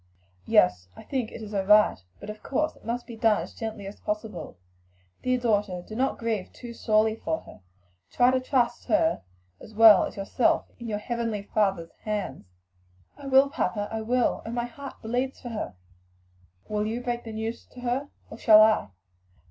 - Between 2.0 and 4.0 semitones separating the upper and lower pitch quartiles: Yes, narrow, 2.6 semitones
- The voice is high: Yes, high, 225 Hz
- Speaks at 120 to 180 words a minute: No, average, 190 wpm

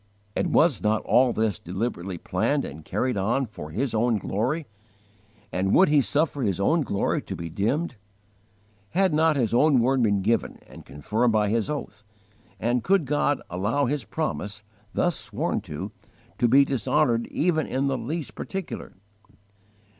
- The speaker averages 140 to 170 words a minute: Yes, average, 160 wpm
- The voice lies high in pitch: No, low, 120 Hz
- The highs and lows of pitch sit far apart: Yes, wide, 6.0 semitones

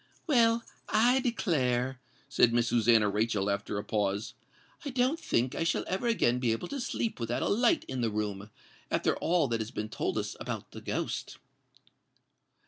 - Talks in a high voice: No, low, 125 Hz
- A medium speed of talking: Yes, average, 175 wpm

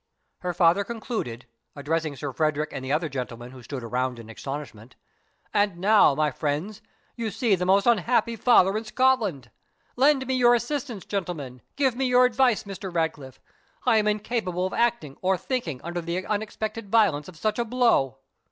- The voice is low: No, high, 190 Hz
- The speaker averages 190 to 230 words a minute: No, average, 170 wpm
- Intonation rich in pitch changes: Yes, wide, 7.9 semitones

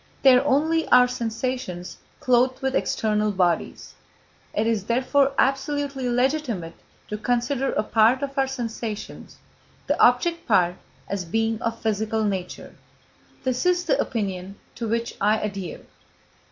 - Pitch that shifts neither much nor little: Yes, average, 4.0 semitones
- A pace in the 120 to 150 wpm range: Yes, slow, 135 wpm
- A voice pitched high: Yes, high, 235 Hz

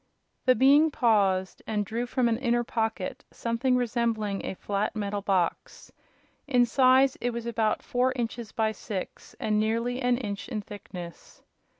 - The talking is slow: No, average, 155 wpm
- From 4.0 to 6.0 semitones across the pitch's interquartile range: No, average, 2.9 semitones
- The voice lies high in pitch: Yes, high, 230 Hz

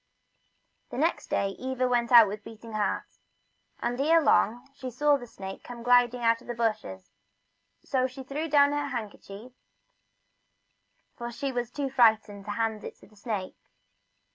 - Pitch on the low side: No, high, 240 Hz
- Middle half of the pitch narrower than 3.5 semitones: Yes, average, 3.1 semitones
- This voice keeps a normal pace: Yes, average, 165 wpm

